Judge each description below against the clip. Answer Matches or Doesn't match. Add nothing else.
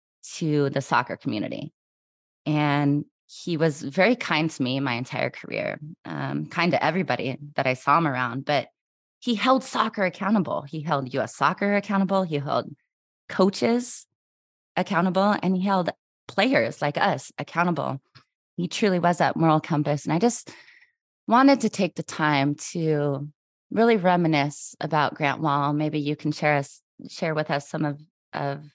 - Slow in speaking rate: Doesn't match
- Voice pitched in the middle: Matches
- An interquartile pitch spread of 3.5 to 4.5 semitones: Doesn't match